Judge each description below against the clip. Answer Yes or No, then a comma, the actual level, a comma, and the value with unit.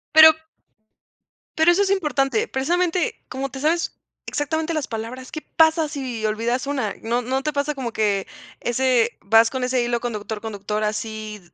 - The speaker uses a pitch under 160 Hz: No, very high, 260 Hz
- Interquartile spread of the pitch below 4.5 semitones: No, wide, 5.6 semitones